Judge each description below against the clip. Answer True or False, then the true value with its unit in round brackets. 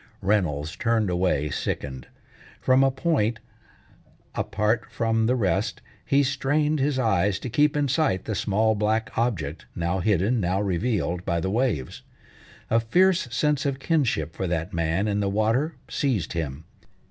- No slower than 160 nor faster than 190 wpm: False (150 wpm)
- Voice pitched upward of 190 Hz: False (110 Hz)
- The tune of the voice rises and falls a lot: True (6.2 semitones)